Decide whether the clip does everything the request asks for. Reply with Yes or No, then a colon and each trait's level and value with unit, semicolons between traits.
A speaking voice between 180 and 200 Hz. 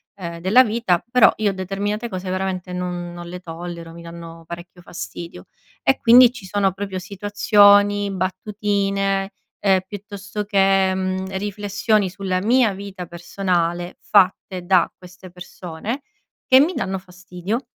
Yes: high, 190 Hz